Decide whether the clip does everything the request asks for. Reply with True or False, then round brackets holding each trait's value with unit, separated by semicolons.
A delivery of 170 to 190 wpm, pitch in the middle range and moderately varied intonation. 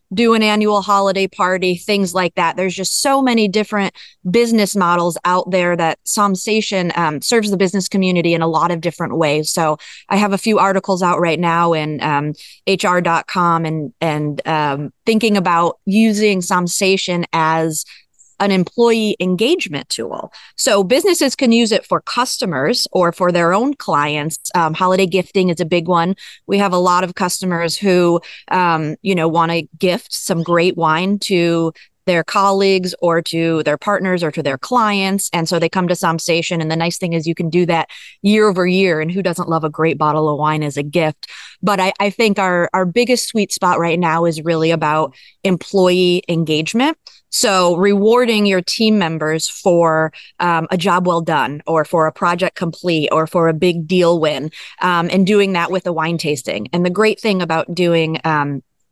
True (185 wpm; 180 Hz; 3.1 semitones)